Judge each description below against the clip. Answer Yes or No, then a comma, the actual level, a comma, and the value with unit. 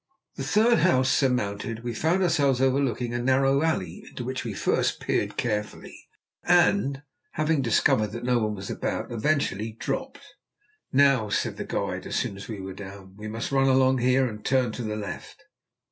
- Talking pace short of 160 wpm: No, average, 175 wpm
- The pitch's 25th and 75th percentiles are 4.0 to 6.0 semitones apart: Yes, average, 4.3 semitones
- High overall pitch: No, low, 125 Hz